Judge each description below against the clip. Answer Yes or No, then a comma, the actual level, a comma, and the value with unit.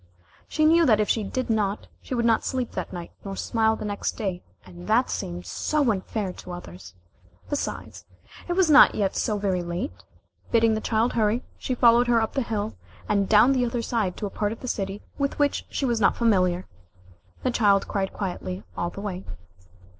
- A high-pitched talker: Yes, high, 215 Hz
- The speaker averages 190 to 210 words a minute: Yes, average, 200 wpm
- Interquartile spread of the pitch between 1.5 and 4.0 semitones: Yes, average, 3.6 semitones